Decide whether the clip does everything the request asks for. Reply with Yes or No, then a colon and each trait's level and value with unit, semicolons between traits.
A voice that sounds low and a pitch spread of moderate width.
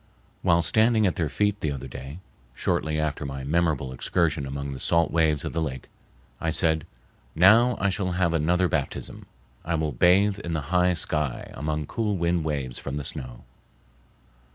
Yes: very low, 80 Hz; average, 4.0 semitones